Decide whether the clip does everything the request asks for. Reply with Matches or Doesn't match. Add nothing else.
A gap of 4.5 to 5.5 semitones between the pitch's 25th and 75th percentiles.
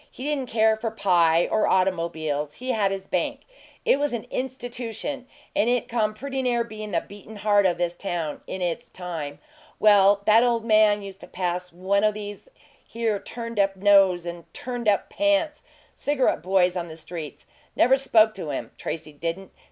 Matches